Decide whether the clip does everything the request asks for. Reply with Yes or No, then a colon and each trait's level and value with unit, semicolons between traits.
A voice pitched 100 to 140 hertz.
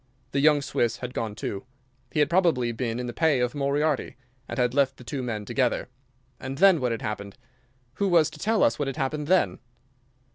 Yes: low, 135 Hz